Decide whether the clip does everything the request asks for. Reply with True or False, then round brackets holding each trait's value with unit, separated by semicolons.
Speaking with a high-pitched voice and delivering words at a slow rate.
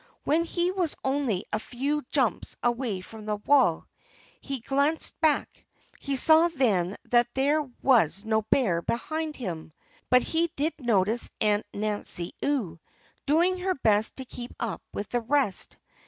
False (250 Hz; 150 wpm)